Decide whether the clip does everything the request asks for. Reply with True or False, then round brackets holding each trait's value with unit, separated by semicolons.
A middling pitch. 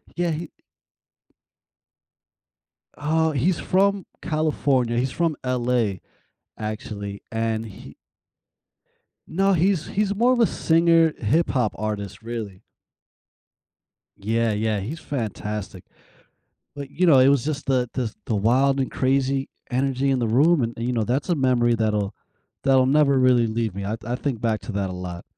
False (125 Hz)